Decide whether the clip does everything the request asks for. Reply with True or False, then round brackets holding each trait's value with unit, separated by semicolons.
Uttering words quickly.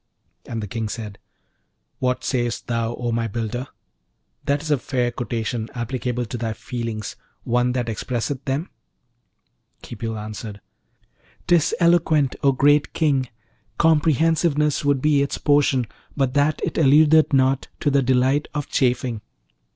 False (135 wpm)